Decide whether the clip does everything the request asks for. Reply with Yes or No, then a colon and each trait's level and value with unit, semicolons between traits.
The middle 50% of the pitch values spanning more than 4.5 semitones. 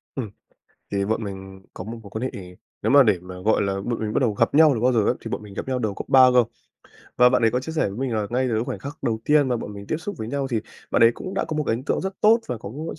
No: average, 4.2 semitones